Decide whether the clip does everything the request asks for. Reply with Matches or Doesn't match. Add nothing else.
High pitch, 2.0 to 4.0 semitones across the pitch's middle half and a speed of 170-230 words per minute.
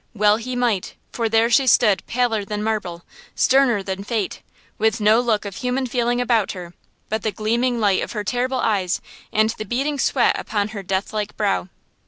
Matches